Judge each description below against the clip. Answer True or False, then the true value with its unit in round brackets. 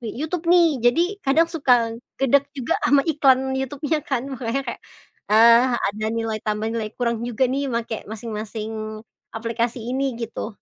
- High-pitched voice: True (240 Hz)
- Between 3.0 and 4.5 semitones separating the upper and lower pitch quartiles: True (3.4 semitones)